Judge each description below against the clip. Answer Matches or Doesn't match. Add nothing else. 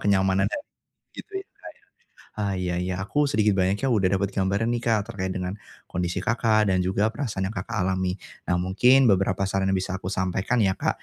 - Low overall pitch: Matches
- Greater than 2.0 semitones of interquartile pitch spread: Matches